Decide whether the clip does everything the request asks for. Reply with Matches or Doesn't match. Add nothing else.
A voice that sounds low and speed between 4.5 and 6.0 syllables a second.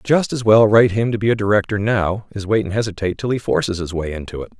Doesn't match